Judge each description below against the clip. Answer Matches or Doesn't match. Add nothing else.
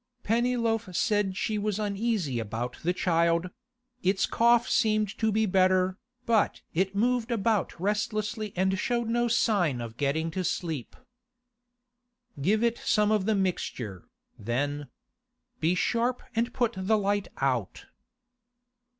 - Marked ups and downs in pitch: Doesn't match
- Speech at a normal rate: Doesn't match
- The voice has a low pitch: Doesn't match